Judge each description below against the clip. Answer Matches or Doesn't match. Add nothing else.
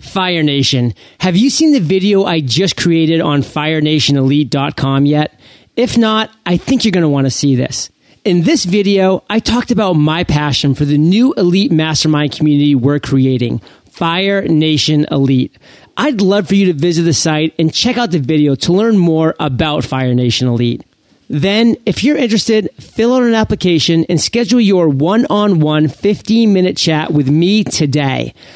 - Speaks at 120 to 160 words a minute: Doesn't match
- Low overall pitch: Doesn't match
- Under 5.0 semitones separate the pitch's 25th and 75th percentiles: Doesn't match